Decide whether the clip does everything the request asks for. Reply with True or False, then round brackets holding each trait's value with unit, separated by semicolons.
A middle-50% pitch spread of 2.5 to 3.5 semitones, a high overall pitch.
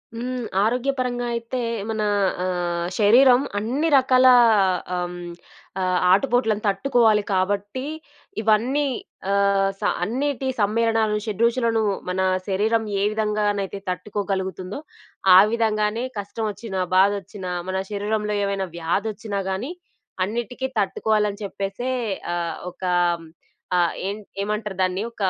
True (3.0 semitones; 210 Hz)